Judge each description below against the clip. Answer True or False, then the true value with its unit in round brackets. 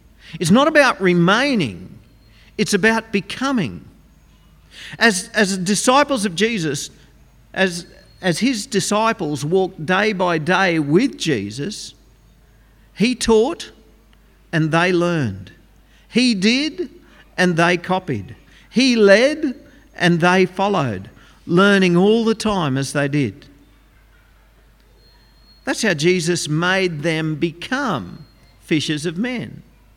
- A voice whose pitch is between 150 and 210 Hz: True (185 Hz)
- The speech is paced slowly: True (105 wpm)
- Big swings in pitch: True (5.7 semitones)